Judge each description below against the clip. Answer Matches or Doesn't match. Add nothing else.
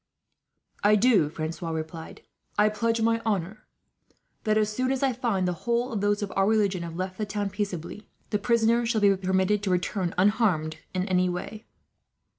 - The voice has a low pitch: Doesn't match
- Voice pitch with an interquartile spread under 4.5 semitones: Matches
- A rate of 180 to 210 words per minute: Matches